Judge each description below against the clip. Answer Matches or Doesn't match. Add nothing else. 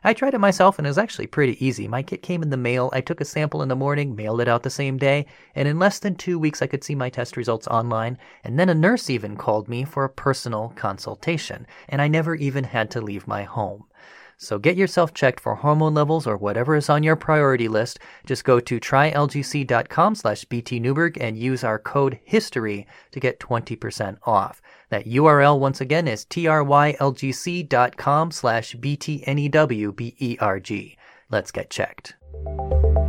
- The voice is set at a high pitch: Doesn't match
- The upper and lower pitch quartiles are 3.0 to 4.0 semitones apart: Doesn't match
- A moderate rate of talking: Matches